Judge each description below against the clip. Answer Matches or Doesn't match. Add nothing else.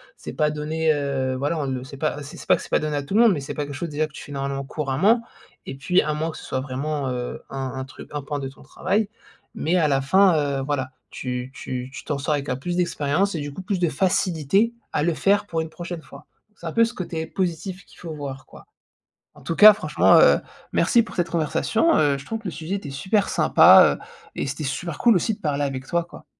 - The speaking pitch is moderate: Matches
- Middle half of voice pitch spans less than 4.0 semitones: Doesn't match